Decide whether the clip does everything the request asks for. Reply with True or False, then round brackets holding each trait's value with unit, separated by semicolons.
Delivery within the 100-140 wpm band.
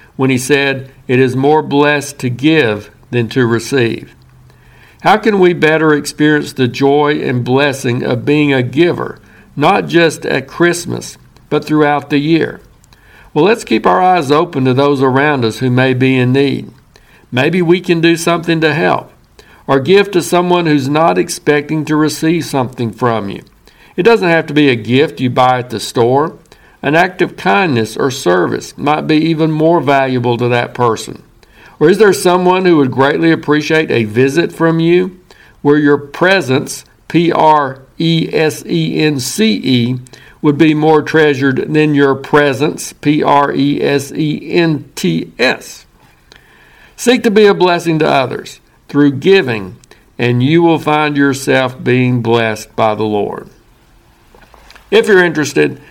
False (165 wpm)